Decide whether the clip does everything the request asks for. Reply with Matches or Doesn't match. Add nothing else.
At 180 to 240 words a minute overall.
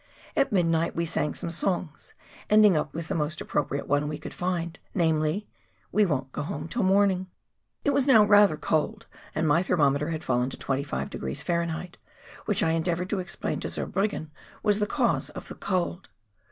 Matches